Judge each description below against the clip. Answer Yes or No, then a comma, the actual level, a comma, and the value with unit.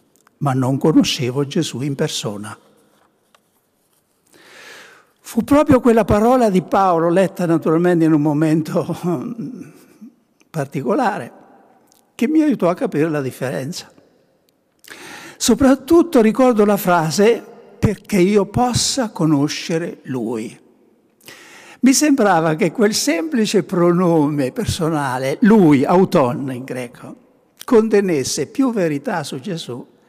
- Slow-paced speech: Yes, slow, 100 wpm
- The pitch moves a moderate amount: No, wide, 7.2 semitones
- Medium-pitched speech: Yes, medium, 180 Hz